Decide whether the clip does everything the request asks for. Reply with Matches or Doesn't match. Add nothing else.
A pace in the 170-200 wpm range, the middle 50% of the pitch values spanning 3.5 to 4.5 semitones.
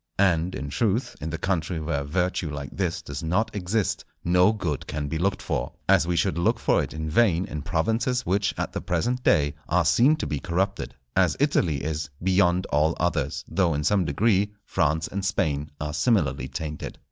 Matches